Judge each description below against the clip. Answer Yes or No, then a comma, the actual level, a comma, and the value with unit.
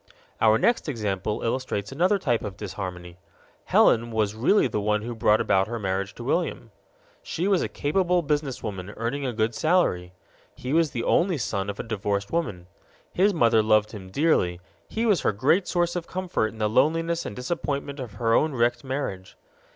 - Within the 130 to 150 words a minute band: No, average, 180 wpm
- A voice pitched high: No, low, 115 Hz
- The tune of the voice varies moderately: No, wide, 7.2 semitones